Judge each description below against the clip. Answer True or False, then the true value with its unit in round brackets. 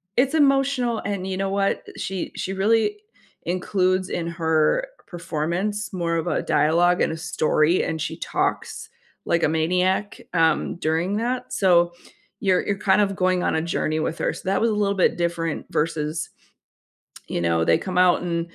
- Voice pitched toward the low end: False (180 Hz)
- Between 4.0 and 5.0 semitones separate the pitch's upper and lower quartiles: False (3.4 semitones)